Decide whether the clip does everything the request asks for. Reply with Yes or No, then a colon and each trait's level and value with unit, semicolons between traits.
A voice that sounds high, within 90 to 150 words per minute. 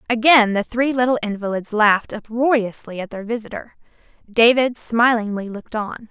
Yes: high, 225 Hz; average, 140 wpm